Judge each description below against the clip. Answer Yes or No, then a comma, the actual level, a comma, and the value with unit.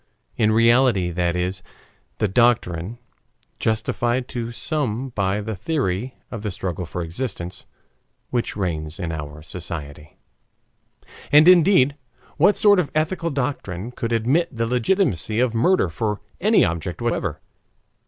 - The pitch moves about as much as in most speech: No, wide, 6.5 semitones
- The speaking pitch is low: Yes, low, 115 Hz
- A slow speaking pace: Yes, slow, 130 wpm